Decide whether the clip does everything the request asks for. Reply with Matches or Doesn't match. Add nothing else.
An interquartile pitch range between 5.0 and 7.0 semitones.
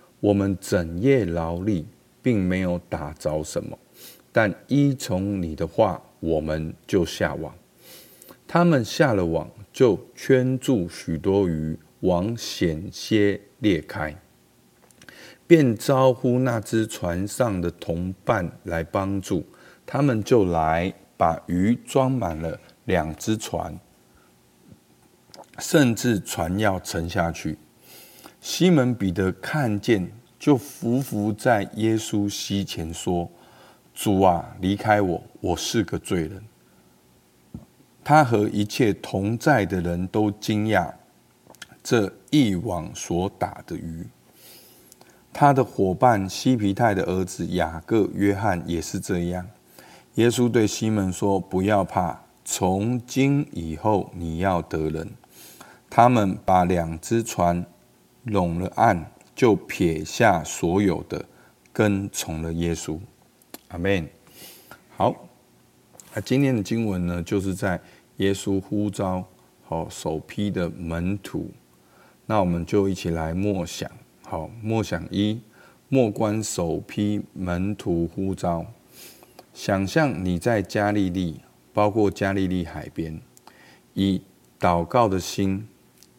Doesn't match